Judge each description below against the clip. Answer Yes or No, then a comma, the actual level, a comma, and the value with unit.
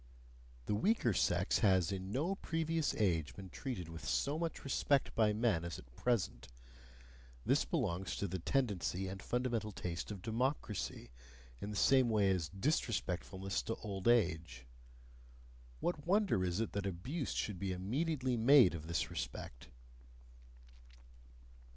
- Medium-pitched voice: No, low, 100 Hz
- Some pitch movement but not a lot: No, wide, 6.2 semitones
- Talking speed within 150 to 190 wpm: No, average, 140 wpm